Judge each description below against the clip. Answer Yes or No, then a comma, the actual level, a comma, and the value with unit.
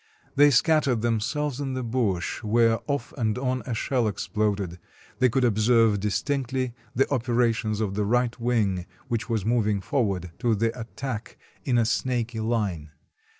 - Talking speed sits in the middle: Yes, average, 150 wpm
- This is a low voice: Yes, low, 115 Hz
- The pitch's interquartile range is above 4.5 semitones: No, average, 3.0 semitones